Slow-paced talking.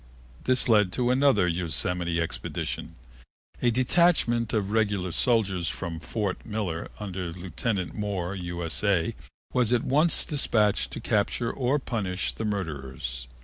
Yes: slow, 125 wpm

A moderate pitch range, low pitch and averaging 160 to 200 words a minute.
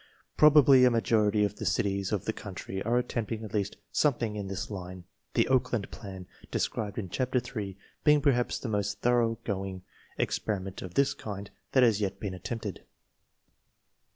Yes: average, 3.7 semitones; low, 105 Hz; average, 175 wpm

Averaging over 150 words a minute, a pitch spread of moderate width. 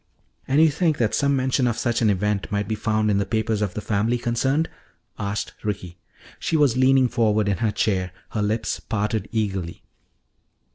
Yes: average, 185 wpm; average, 3.6 semitones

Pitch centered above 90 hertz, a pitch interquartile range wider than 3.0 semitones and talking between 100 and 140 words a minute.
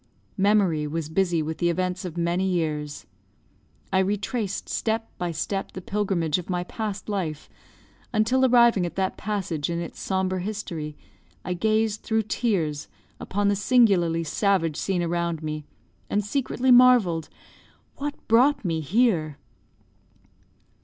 Yes: high, 190 Hz; average, 4.4 semitones; slow, 135 wpm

